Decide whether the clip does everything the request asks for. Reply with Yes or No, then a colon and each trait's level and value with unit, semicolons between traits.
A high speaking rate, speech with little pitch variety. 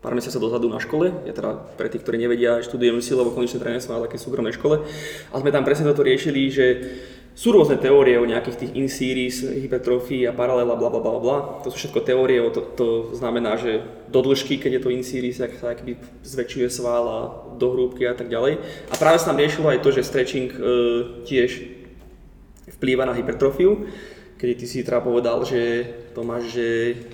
Yes: fast, 200 wpm; narrow, 1.8 semitones